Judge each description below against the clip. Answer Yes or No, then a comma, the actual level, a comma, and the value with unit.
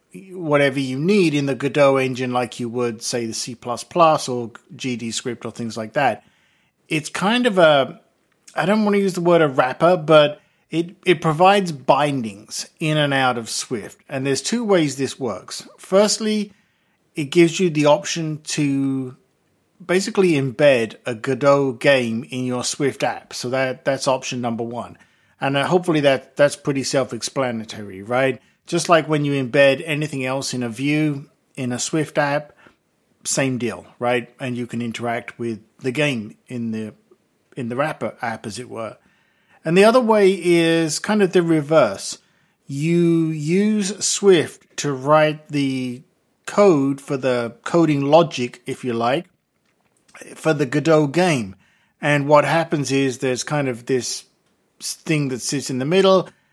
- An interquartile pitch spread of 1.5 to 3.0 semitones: No, average, 4.7 semitones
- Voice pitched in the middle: Yes, medium, 145 Hz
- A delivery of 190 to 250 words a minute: No, average, 160 wpm